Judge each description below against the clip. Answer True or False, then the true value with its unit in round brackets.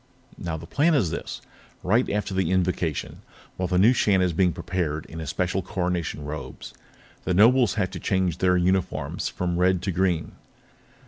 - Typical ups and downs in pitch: False (1.9 semitones)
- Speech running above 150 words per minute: True (175 wpm)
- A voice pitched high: False (90 Hz)